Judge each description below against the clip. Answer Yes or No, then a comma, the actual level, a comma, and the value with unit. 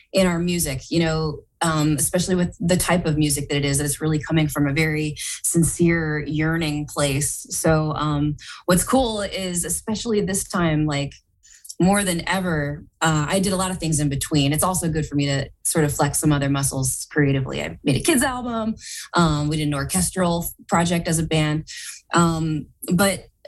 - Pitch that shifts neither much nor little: Yes, average, 3.3 semitones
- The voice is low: No, medium, 160 Hz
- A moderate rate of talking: No, fast, 190 wpm